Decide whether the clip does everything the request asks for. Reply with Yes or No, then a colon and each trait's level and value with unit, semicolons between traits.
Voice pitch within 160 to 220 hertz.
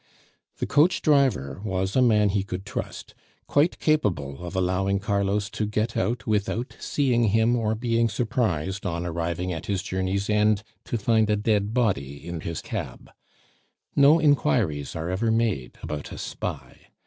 No: low, 105 Hz